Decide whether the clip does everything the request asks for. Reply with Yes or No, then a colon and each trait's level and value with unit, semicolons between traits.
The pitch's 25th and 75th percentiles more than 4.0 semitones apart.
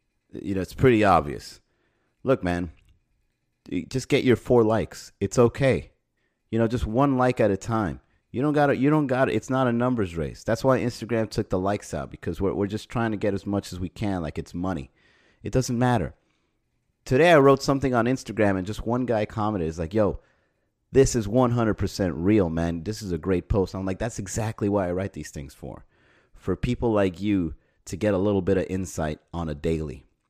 Yes: average, 4.6 semitones